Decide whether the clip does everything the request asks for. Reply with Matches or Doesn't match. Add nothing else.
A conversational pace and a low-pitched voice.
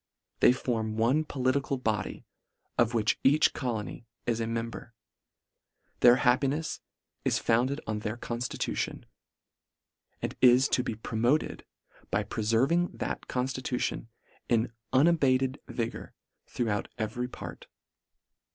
Doesn't match